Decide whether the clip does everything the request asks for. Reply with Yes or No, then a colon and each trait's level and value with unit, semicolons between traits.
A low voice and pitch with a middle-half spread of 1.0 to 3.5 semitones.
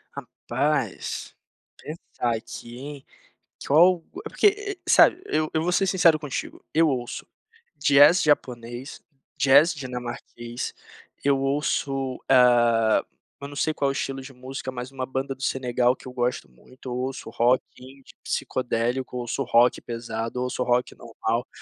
Yes: low, 130 Hz; average, 2.8 semitones